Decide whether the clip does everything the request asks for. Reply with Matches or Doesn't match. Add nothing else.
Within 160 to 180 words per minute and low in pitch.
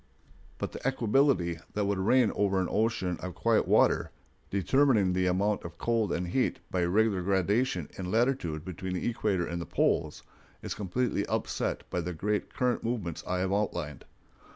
Matches